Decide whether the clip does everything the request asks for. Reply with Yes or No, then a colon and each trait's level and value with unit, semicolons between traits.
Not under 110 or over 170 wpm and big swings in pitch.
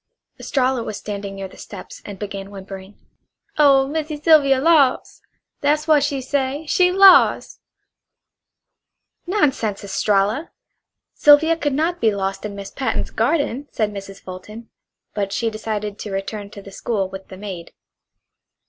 Yes: average, 140 wpm; wide, 6.5 semitones